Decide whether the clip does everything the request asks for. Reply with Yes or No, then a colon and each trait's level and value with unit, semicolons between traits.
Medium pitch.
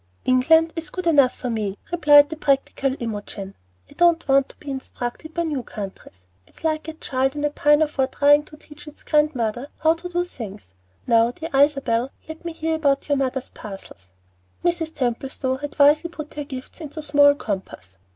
No: very high, 285 Hz